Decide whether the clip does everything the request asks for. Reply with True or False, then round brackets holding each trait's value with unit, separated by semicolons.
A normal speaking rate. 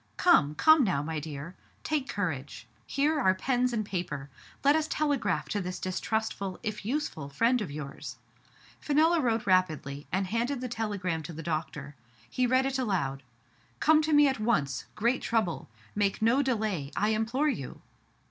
True (170 wpm)